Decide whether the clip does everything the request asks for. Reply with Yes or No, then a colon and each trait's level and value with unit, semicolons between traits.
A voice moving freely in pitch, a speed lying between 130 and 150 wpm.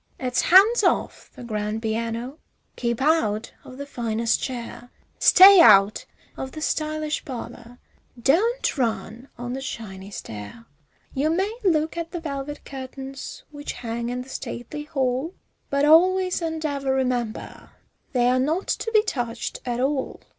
No: average, 4.7 semitones; average, 145 wpm